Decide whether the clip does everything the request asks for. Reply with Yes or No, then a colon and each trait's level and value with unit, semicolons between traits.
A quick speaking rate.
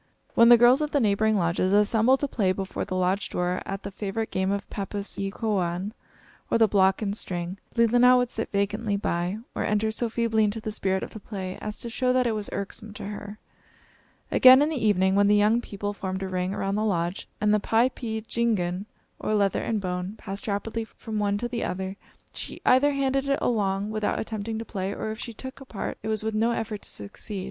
Yes: fast, 220 wpm